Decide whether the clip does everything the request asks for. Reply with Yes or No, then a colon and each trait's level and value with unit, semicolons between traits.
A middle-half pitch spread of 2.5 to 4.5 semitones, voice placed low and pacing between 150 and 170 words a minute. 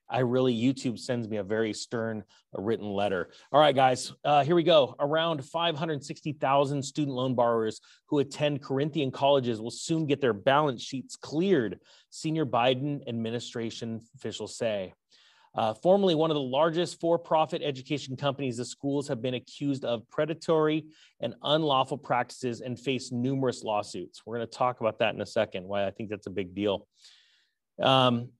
Yes: average, 4.0 semitones; low, 130 Hz; average, 165 wpm